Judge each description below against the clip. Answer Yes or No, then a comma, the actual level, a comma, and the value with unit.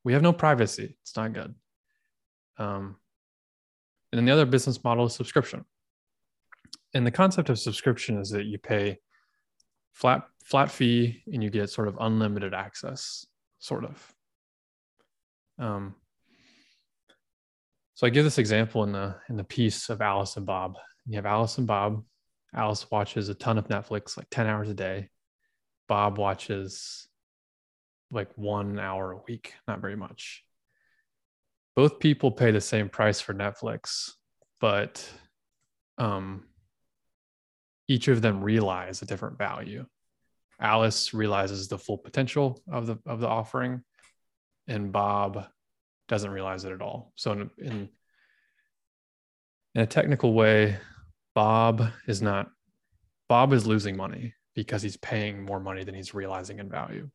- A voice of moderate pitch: No, low, 105 Hz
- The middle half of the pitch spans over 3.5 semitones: No, average, 3.2 semitones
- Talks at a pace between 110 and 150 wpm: Yes, average, 145 wpm